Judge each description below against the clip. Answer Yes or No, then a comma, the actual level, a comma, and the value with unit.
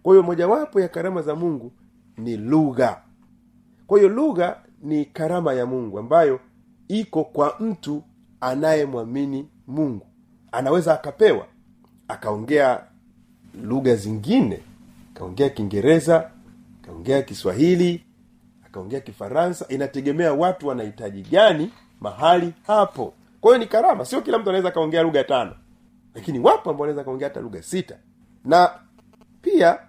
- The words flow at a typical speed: Yes, average, 120 wpm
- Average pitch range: No, wide, 8.2 semitones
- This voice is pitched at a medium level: Yes, medium, 165 Hz